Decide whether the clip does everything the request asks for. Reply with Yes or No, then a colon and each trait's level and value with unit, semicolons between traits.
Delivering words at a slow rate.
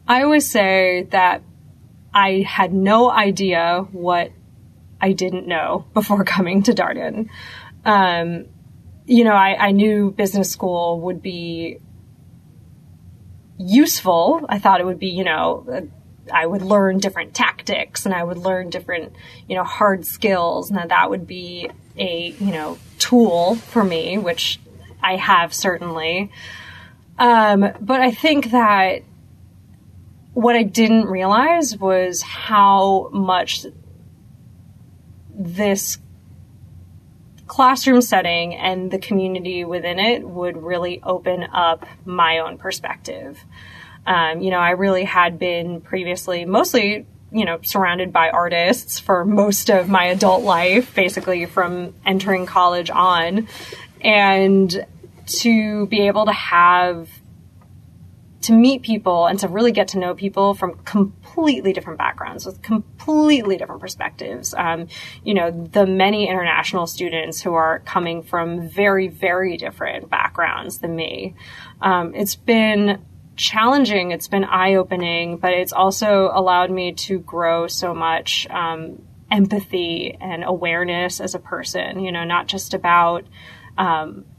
Yes: slow, 130 wpm